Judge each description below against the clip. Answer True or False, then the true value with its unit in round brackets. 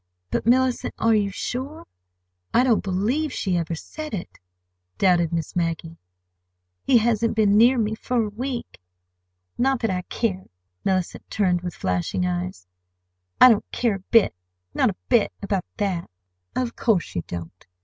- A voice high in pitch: True (200 Hz)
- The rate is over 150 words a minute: False (145 wpm)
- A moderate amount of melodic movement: False (5.7 semitones)